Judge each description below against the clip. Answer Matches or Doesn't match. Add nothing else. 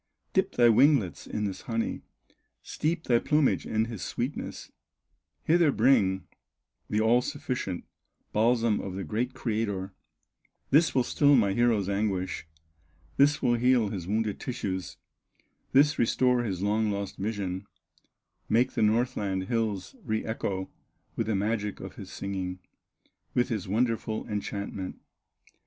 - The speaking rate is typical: Doesn't match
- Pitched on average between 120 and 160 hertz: Doesn't match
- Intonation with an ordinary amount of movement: Matches